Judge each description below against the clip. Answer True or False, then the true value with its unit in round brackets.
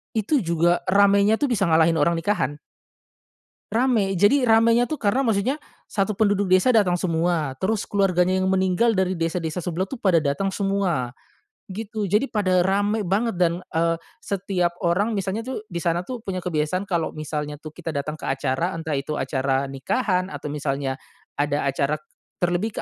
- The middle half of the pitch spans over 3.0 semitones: True (3.9 semitones)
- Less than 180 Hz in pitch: False (185 Hz)